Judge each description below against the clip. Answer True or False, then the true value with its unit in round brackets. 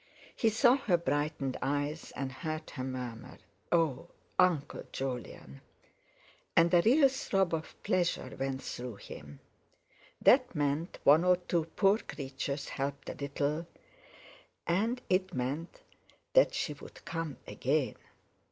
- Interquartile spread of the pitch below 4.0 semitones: False (5.1 semitones)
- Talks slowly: True (125 wpm)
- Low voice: False (155 Hz)